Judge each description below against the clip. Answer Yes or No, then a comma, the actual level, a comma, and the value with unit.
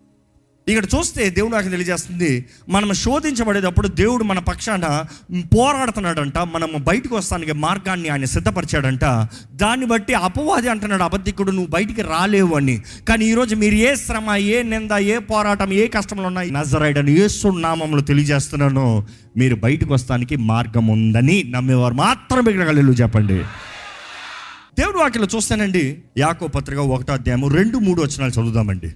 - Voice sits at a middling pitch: Yes, medium, 170 Hz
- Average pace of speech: No, fast, 130 wpm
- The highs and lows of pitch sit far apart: Yes, wide, 7.8 semitones